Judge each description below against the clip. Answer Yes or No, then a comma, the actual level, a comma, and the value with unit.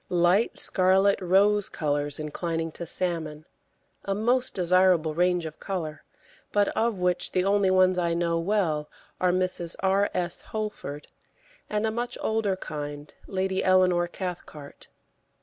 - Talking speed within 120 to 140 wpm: Yes, slow, 135 wpm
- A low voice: No, medium, 180 Hz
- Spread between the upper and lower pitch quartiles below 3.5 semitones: Yes, average, 2.9 semitones